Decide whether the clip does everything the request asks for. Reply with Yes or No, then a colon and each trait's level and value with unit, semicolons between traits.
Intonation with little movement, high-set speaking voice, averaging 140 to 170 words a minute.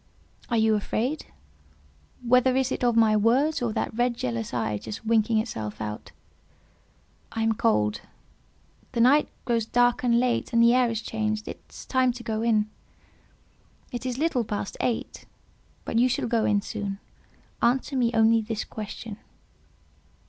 Yes: narrow, 2.2 semitones; high, 230 Hz; average, 160 wpm